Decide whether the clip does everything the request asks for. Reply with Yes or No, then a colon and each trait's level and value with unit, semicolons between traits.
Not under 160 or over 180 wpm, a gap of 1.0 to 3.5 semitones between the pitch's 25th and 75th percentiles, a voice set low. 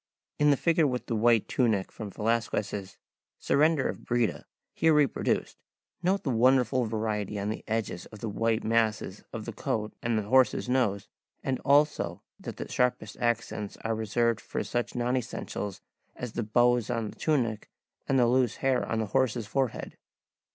Yes: average, 170 wpm; average, 3.1 semitones; low, 115 Hz